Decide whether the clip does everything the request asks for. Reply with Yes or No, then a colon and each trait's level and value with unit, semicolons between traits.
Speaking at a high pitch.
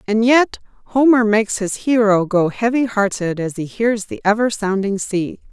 Yes: high, 215 Hz